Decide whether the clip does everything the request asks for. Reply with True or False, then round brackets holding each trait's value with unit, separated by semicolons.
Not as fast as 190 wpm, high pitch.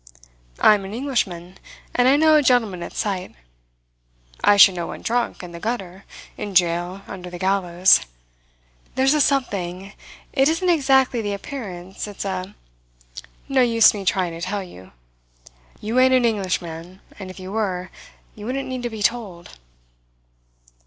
True (160 wpm; 200 Hz)